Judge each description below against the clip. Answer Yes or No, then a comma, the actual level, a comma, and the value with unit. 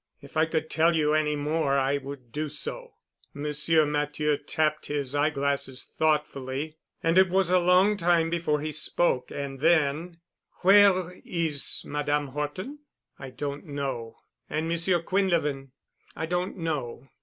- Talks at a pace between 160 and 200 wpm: No, average, 145 wpm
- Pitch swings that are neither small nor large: Yes, average, 3.0 semitones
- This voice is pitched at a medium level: Yes, medium, 150 Hz